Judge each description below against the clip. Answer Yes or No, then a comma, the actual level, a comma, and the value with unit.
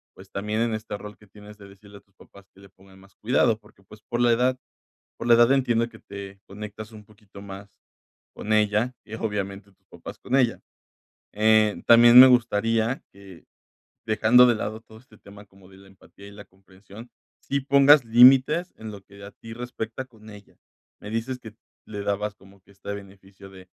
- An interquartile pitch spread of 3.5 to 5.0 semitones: No, average, 2.7 semitones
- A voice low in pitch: Yes, low, 105 Hz